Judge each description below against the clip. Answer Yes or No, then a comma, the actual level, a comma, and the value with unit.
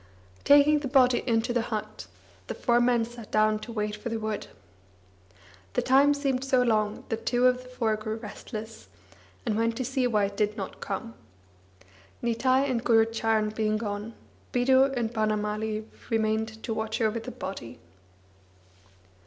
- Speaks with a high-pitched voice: Yes, high, 225 Hz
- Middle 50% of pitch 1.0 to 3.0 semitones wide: Yes, narrow, 2.5 semitones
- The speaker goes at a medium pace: Yes, average, 160 wpm